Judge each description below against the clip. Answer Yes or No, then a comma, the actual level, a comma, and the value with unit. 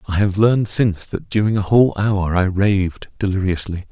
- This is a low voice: Yes, low, 100 Hz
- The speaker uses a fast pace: No, average, 185 wpm